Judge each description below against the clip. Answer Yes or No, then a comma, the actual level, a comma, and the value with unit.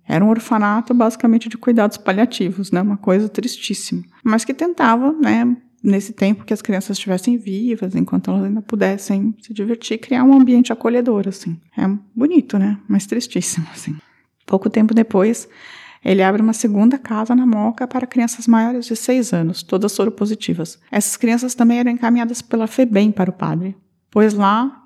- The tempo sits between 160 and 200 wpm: Yes, average, 170 wpm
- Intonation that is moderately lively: Yes, average, 3.3 semitones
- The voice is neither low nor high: No, high, 220 Hz